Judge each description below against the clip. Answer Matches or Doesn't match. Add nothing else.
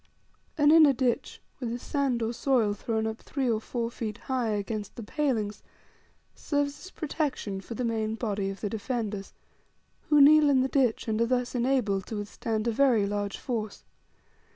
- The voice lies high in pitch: Matches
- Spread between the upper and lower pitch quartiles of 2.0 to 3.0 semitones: Doesn't match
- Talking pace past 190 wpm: Doesn't match